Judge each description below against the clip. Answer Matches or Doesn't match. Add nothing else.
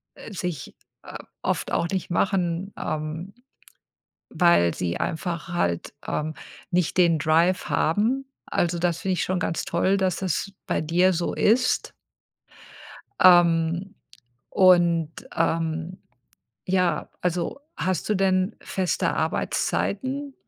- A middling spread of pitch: Doesn't match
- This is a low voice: Doesn't match